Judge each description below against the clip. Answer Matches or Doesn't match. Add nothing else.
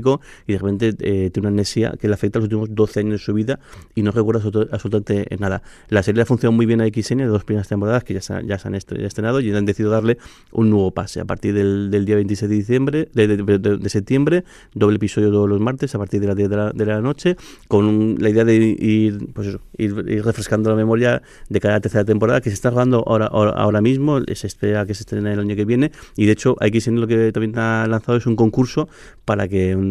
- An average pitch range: Doesn't match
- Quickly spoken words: Matches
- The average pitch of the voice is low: Matches